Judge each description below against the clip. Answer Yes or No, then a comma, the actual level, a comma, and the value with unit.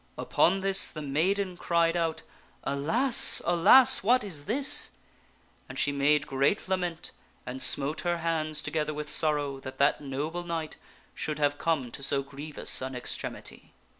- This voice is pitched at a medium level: Yes, medium, 155 Hz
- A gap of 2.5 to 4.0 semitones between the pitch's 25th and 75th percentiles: Yes, average, 3.7 semitones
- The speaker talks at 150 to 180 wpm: Yes, average, 155 wpm